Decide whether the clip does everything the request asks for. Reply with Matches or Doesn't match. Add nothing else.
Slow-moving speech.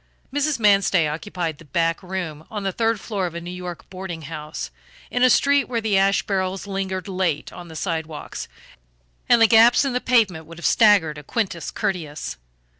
Doesn't match